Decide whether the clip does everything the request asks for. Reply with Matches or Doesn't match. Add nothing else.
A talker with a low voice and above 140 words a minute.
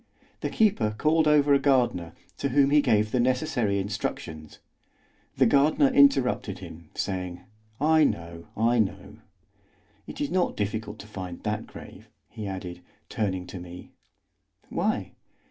Doesn't match